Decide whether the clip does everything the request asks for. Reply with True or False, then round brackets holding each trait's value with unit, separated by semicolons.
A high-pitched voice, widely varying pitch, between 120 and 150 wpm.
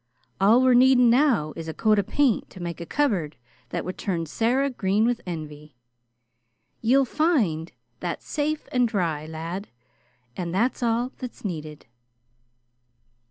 True (210 Hz; 7.1 semitones; 145 wpm)